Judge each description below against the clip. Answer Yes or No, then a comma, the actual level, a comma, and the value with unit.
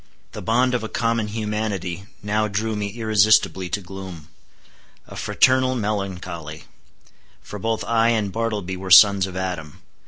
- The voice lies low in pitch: Yes, low, 105 Hz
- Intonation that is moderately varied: Yes, average, 3.0 semitones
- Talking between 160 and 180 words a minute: No, average, 145 wpm